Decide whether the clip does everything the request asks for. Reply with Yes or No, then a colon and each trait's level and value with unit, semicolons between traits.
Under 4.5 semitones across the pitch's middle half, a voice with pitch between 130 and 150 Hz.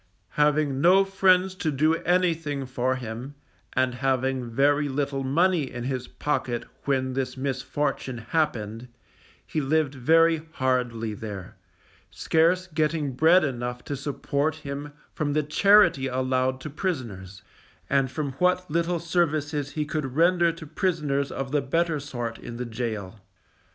Yes: average, 3.7 semitones; medium, 140 Hz